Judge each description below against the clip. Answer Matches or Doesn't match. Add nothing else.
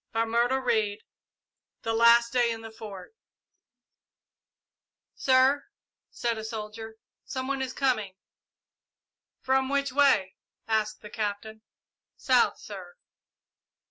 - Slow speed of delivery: Matches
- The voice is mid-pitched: Doesn't match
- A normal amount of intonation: Matches